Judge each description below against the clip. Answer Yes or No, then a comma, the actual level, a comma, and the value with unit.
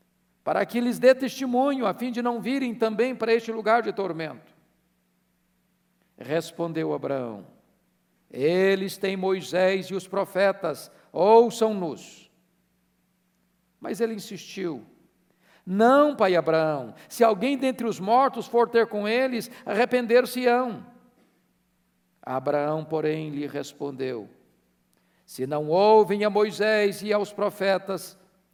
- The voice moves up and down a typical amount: No, wide, 6.7 semitones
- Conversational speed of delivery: No, slow, 110 wpm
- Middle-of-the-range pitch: No, high, 195 Hz